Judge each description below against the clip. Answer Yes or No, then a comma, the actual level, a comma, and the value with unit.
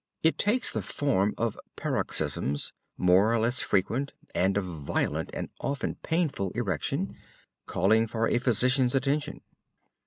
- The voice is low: Yes, low, 115 Hz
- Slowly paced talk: Yes, slow, 130 wpm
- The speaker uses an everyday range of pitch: No, wide, 6.0 semitones